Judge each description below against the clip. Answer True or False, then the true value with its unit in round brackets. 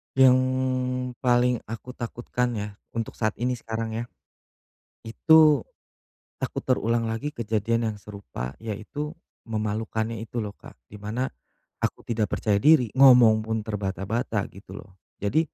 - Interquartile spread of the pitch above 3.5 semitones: False (2.7 semitones)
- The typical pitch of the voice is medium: False (115 Hz)